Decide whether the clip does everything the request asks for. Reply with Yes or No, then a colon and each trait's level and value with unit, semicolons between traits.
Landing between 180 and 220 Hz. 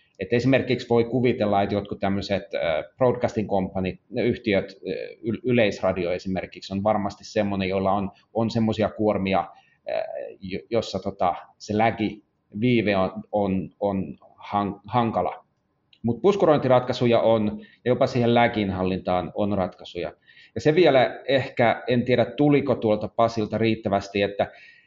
No: low, 105 Hz